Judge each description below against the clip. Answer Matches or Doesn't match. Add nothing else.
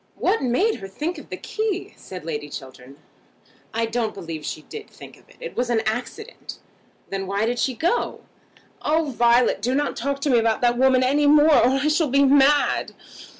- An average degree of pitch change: Matches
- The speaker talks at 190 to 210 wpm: Matches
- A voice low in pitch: Doesn't match